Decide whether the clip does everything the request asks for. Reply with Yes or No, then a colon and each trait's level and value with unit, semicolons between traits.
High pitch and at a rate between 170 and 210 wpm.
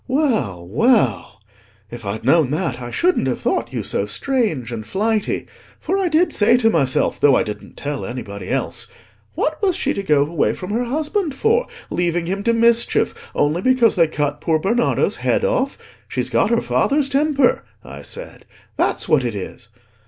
Yes: high, 195 Hz; average, 180 wpm